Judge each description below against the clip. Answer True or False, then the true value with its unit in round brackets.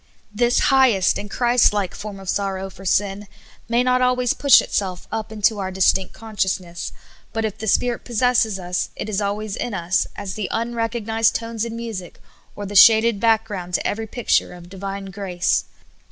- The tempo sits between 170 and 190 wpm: True (180 wpm)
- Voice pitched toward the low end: False (210 Hz)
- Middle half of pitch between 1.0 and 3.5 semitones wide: True (3.0 semitones)